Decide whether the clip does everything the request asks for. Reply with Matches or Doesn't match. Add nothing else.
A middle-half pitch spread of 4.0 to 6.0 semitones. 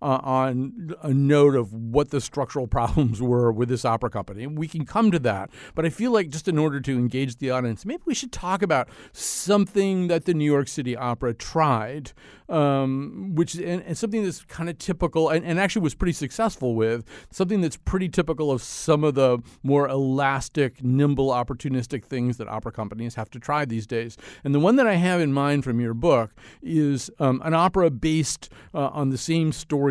Matches